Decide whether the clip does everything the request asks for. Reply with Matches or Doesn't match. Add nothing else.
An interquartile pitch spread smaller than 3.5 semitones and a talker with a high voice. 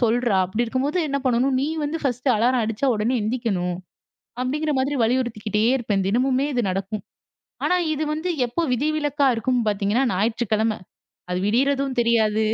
Doesn't match